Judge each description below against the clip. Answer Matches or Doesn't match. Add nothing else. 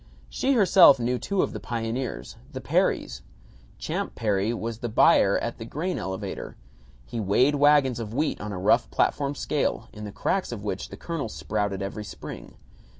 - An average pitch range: Doesn't match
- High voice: Doesn't match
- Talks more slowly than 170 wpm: Doesn't match